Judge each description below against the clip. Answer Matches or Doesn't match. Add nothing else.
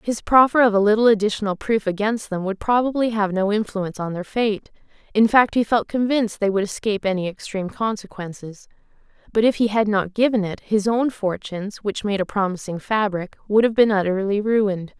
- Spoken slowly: Doesn't match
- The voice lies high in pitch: Matches